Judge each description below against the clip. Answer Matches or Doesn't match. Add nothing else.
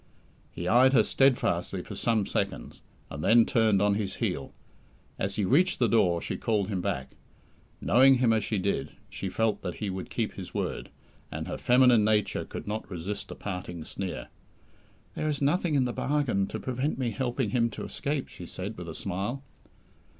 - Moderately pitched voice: Doesn't match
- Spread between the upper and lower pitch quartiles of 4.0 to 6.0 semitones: Matches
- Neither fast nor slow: Matches